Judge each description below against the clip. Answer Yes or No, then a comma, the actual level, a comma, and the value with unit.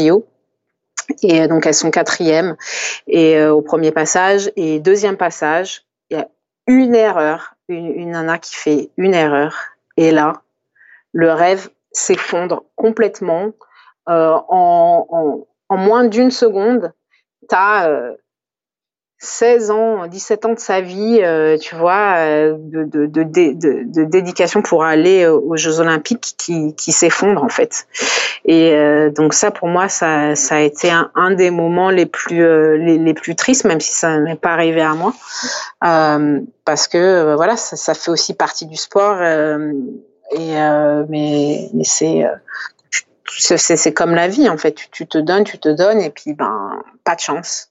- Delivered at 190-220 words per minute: No, average, 165 wpm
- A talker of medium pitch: Yes, medium, 165 Hz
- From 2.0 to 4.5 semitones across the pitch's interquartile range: Yes, average, 4.2 semitones